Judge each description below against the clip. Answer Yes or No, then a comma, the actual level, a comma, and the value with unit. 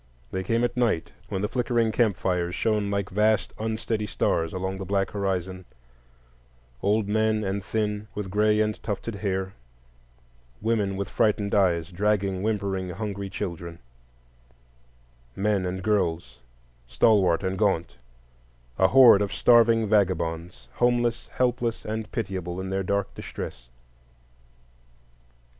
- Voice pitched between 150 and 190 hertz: No, low, 100 Hz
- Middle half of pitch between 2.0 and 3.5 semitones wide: Yes, average, 2.8 semitones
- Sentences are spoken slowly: Yes, slow, 125 wpm